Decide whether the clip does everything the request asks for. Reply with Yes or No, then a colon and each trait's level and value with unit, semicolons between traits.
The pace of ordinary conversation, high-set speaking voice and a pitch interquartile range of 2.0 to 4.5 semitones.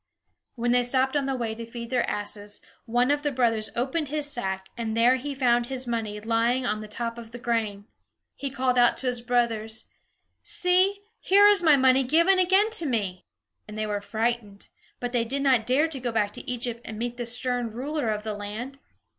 No: fast, 210 wpm; high, 240 Hz; average, 3.1 semitones